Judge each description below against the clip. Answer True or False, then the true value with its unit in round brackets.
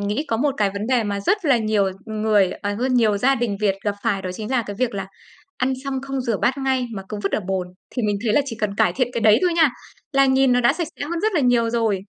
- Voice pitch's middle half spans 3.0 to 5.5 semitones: True (4.4 semitones)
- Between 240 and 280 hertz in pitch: False (230 Hz)